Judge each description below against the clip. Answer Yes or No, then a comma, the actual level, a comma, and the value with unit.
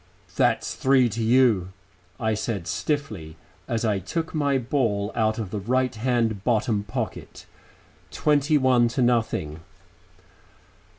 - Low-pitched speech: Yes, low, 115 Hz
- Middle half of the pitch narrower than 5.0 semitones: Yes, average, 3.8 semitones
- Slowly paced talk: Yes, slow, 125 wpm